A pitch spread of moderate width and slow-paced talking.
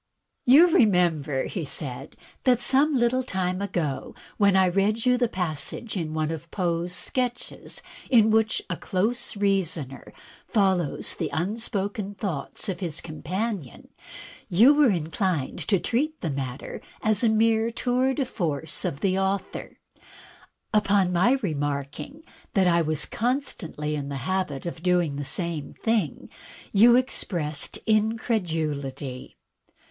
No: wide, 6.3 semitones; slow, 130 wpm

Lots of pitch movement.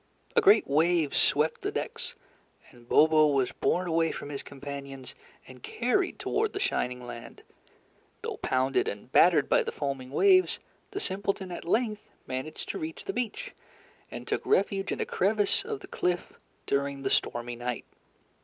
Yes: wide, 6.7 semitones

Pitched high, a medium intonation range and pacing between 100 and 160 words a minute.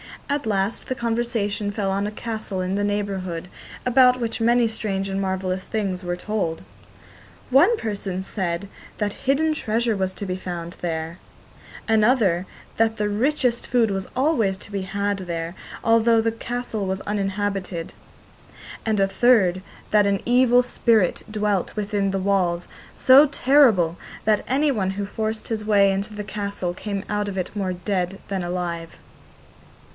Yes: high, 205 Hz; average, 3.1 semitones; average, 155 wpm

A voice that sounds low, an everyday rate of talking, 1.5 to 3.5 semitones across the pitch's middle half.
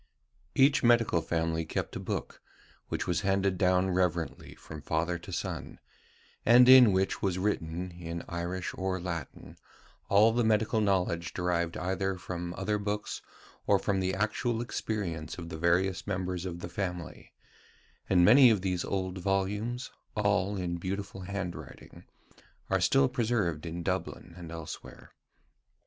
Yes: very low, 95 Hz; average, 145 wpm; average, 3.0 semitones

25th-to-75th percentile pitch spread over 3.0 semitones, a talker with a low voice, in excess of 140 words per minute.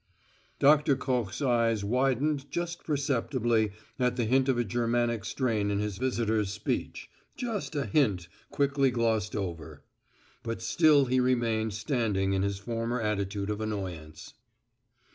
No: average, 4.2 semitones; low, 115 Hz; slow, 135 wpm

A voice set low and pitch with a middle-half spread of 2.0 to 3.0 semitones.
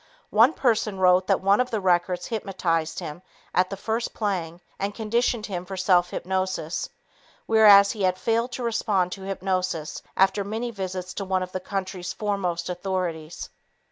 No: high, 190 Hz; narrow, 2.6 semitones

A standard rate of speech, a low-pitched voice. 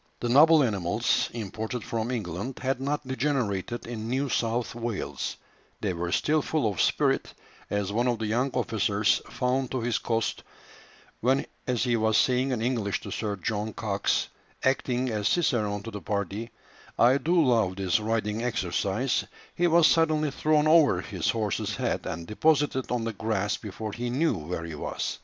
Yes: average, 170 wpm; low, 115 Hz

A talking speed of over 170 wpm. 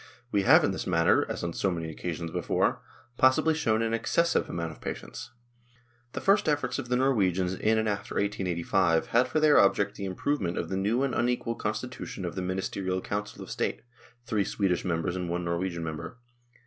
Yes: average, 190 wpm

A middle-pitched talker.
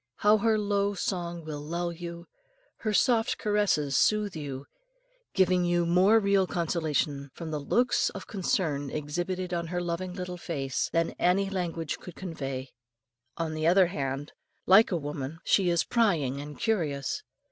Yes: medium, 175 Hz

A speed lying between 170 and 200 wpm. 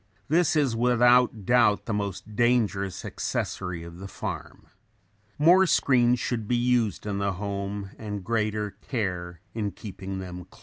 No: average, 145 wpm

